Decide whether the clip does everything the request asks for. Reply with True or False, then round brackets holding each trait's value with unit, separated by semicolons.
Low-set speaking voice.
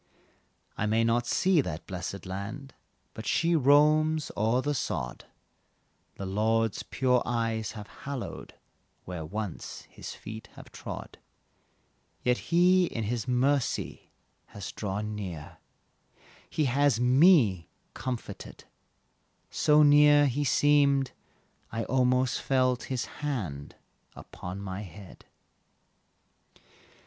True (120 Hz)